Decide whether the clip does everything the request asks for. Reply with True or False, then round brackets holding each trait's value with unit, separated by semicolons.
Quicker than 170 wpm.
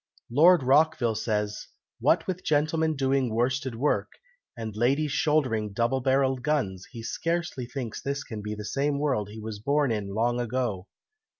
False (160 wpm)